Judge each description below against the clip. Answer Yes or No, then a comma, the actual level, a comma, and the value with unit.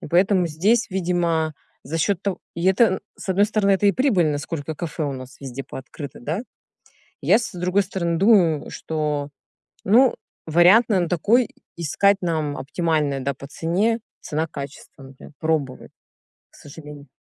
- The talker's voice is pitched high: No, medium, 170 Hz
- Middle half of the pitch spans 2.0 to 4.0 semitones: No, average, 4.7 semitones